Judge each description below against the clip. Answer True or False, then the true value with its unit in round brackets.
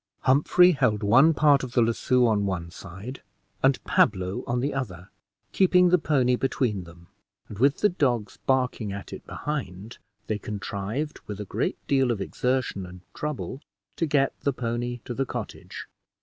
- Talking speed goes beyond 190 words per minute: False (165 wpm)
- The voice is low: True (125 Hz)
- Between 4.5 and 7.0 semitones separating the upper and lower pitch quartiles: True (5.1 semitones)